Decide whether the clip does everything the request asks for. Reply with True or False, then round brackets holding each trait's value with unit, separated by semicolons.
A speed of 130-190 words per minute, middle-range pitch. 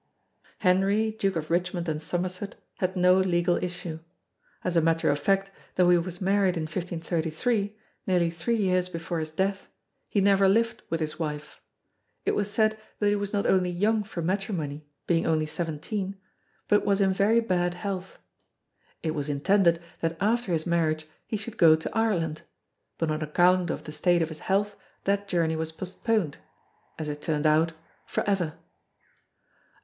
True (170 wpm; 180 Hz)